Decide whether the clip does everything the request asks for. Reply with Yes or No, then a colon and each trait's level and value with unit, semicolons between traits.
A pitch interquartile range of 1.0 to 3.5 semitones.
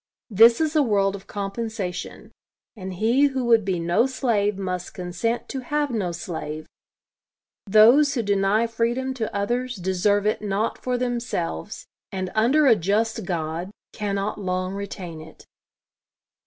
No: average, 4.1 semitones